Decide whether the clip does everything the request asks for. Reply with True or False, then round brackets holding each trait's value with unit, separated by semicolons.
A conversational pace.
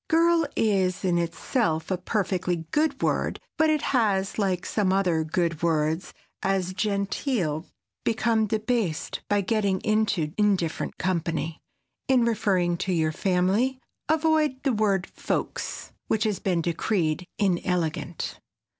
False (125 wpm)